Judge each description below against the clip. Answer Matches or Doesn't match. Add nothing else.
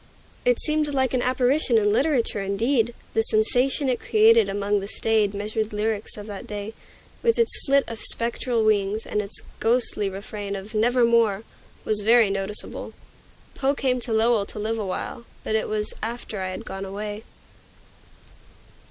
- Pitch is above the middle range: Matches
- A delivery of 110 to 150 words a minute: Doesn't match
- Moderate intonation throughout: Matches